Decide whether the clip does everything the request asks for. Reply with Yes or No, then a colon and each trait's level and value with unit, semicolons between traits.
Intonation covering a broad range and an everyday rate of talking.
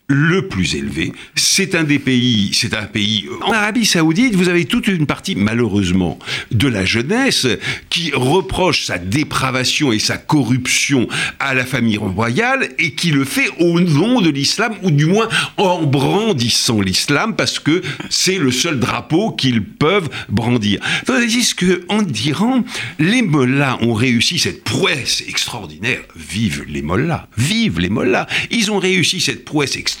Yes: wide, 7.8 semitones; average, 160 wpm